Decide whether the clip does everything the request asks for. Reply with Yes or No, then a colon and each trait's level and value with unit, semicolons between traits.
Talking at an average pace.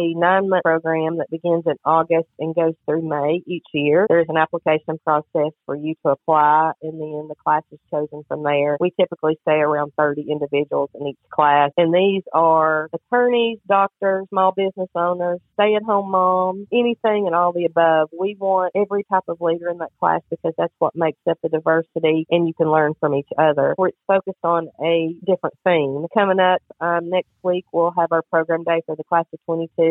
Yes: average, 195 wpm